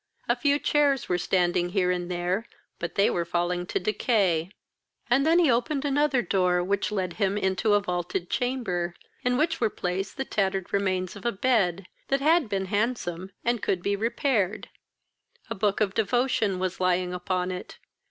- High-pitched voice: Yes, high, 195 Hz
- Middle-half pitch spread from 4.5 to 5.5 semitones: Yes, average, 5.1 semitones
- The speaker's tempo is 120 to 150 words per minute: No, average, 170 wpm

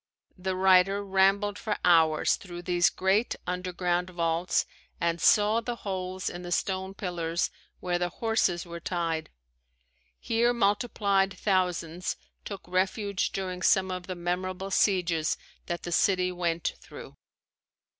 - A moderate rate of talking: No, slow, 130 wpm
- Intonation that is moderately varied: No, narrow, 2.0 semitones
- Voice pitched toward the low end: No, medium, 185 Hz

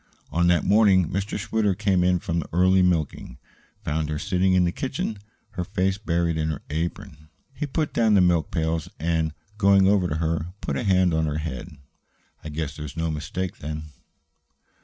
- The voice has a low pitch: Yes, very low, 85 Hz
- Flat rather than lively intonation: No, average, 3.3 semitones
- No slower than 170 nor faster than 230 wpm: Yes, average, 185 wpm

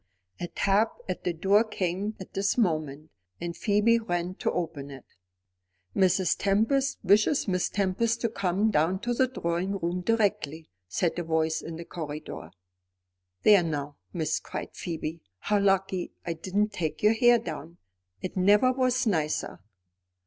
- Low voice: No, medium, 185 Hz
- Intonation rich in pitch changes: No, average, 4.2 semitones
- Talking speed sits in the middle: Yes, average, 150 wpm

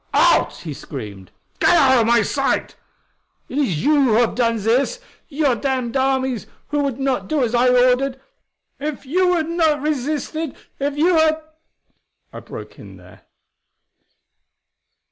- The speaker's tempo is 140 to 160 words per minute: Yes, average, 150 wpm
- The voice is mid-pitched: No, very high, 270 Hz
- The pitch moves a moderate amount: Yes, average, 3.8 semitones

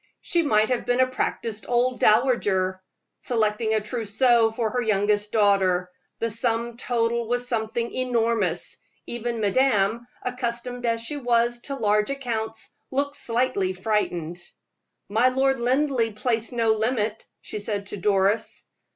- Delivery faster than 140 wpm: No, slow, 135 wpm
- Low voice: No, high, 230 Hz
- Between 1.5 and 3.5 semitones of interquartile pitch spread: Yes, average, 2.7 semitones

